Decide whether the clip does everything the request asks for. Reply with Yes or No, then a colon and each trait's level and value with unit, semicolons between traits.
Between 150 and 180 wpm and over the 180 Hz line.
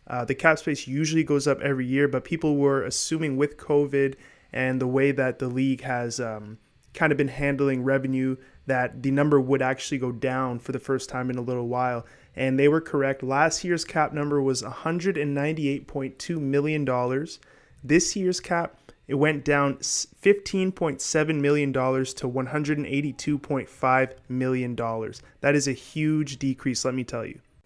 No: average, 160 wpm; medium, 140 Hz